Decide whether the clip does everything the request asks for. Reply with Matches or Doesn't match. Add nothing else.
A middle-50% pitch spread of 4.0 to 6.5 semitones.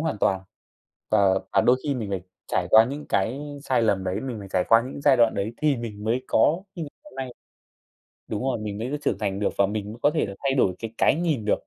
Matches